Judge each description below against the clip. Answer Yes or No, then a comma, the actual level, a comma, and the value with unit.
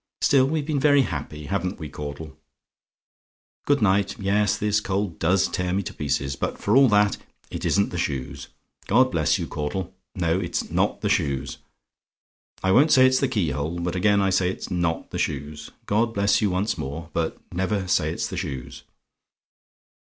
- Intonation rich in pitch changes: No, average, 4.6 semitones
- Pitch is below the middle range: Yes, very low, 95 Hz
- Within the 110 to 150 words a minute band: No, average, 180 wpm